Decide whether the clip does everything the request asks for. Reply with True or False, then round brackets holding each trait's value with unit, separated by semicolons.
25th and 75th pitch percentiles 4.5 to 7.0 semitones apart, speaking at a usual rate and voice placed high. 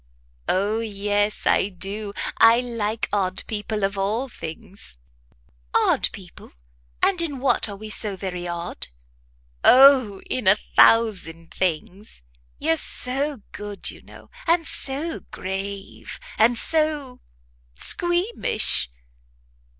False (4.8 semitones; 110 wpm; 210 Hz)